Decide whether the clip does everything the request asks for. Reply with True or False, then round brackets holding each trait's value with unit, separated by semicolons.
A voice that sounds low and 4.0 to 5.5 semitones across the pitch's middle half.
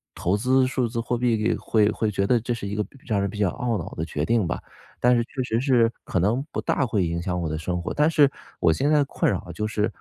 True (110 Hz; 4.3 semitones)